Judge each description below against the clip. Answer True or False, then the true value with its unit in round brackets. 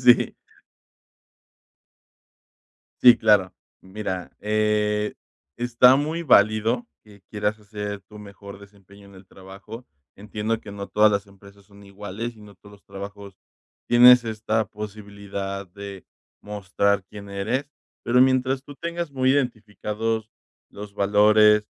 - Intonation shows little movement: True (2.1 semitones)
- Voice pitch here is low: True (105 Hz)